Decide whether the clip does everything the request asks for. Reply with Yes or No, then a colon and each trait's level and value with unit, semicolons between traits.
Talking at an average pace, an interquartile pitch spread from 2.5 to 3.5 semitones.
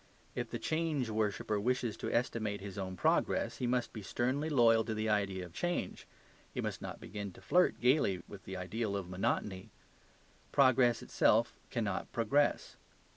No: average, 165 wpm; average, 3.9 semitones